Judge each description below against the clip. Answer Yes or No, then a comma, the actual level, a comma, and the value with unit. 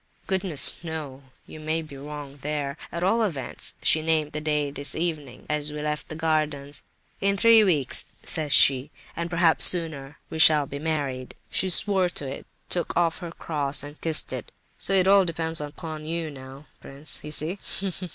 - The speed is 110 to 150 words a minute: No, average, 175 wpm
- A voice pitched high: No, medium, 155 Hz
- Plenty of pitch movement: No, average, 2.7 semitones